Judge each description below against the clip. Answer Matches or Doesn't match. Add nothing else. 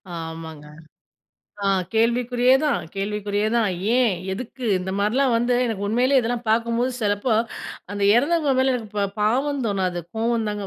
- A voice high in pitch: Matches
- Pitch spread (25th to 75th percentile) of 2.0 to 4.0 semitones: Matches